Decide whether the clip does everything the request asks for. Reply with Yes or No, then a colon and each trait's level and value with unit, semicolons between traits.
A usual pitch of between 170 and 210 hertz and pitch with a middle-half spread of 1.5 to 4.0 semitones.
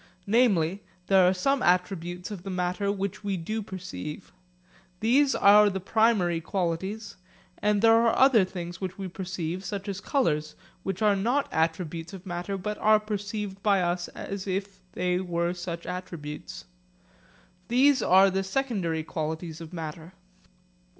Yes: high, 190 Hz; average, 3.1 semitones